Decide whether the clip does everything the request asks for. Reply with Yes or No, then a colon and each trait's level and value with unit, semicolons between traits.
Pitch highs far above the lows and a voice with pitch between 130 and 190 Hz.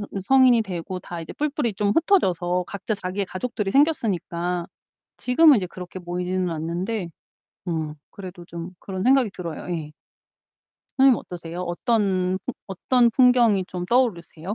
No: average, 5.0 semitones; medium, 185 Hz